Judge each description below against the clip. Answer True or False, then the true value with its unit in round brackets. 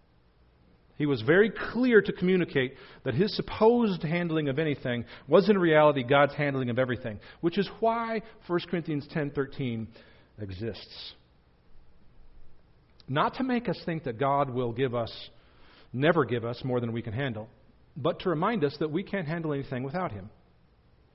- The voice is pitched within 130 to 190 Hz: True (140 Hz)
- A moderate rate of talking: True (160 wpm)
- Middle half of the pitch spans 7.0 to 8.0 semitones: True (7.3 semitones)